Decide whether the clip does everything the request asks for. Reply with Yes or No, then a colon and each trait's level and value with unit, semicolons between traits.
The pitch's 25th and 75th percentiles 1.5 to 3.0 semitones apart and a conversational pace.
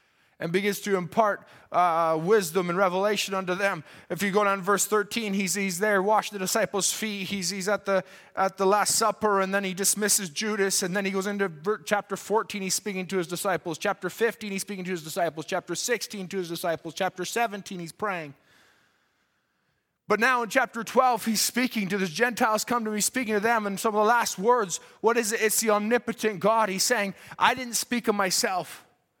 No: narrow, 2.5 semitones; fast, 210 wpm